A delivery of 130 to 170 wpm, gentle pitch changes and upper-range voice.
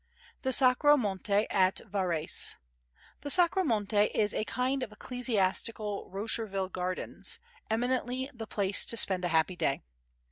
No: slow, 135 wpm; average, 4.7 semitones; high, 215 Hz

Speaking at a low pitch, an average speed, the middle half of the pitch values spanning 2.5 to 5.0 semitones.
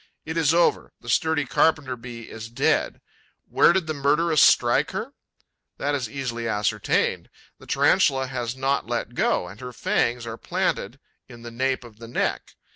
Yes: low, 130 Hz; average, 170 wpm; average, 3.7 semitones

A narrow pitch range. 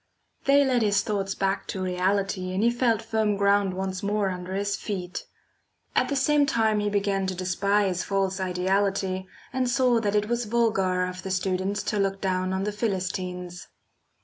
Yes: narrow, 2.2 semitones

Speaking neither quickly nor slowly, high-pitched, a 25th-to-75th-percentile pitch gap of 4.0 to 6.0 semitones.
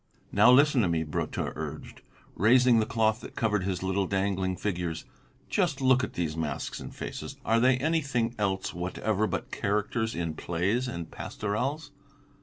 No: average, 160 wpm; low, 105 Hz; average, 5.2 semitones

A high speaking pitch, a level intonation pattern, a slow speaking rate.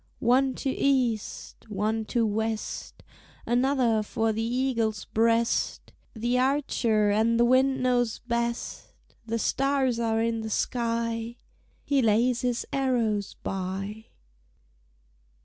Yes: high, 230 Hz; narrow, 2.3 semitones; slow, 115 wpm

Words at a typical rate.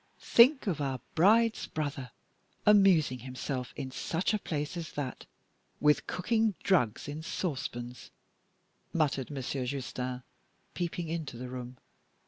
No: slow, 120 wpm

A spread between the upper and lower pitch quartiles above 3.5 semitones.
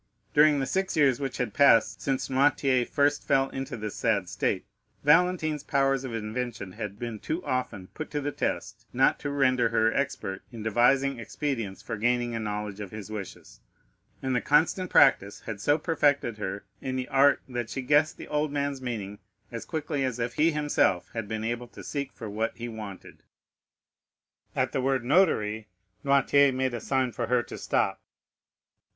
Yes: average, 4.1 semitones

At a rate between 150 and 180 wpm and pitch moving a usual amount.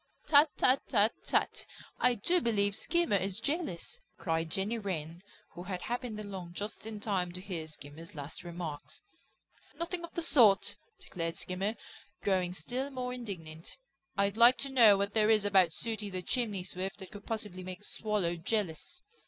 Yes: average, 170 wpm; average, 4.4 semitones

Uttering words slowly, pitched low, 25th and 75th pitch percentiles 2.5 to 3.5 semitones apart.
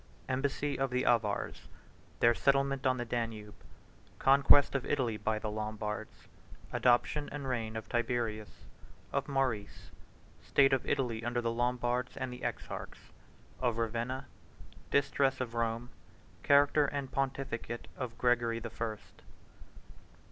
Yes: slow, 105 wpm; low, 120 Hz; average, 2.8 semitones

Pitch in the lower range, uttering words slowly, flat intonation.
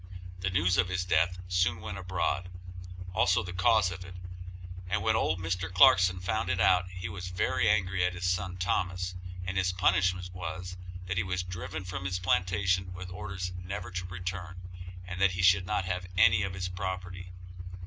No: very low, 90 Hz; average, 185 wpm; narrow, 0.5 semitones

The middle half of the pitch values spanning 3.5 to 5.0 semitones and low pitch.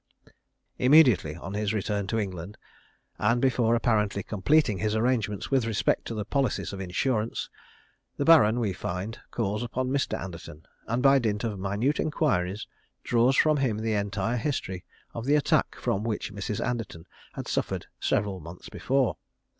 Yes: average, 4.1 semitones; low, 110 Hz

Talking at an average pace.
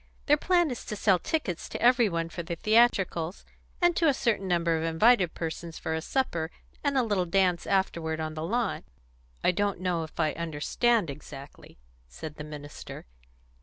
Yes: average, 180 wpm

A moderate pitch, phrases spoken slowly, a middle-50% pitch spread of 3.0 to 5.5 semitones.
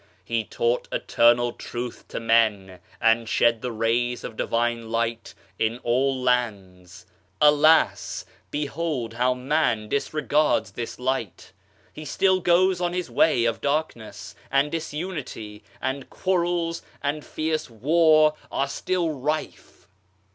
No: low, 130 Hz; slow, 120 wpm; average, 5.1 semitones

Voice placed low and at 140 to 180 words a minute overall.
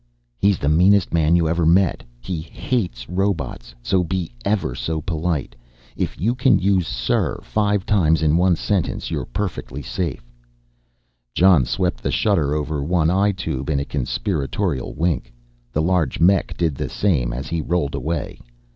Yes: very low, 85 Hz; average, 160 wpm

